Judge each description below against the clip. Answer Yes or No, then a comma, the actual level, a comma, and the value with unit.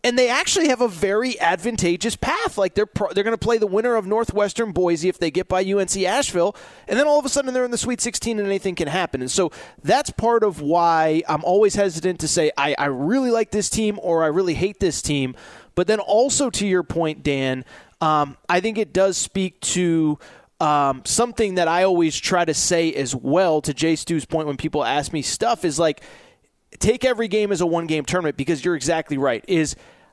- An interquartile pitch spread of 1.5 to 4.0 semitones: No, average, 5.3 semitones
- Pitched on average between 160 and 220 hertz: Yes, medium, 185 Hz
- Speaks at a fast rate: Yes, fast, 220 wpm